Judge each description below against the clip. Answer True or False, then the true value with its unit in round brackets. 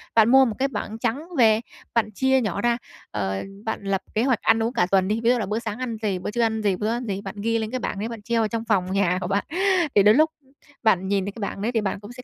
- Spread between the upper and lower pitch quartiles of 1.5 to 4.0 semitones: True (2.8 semitones)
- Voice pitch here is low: False (220 Hz)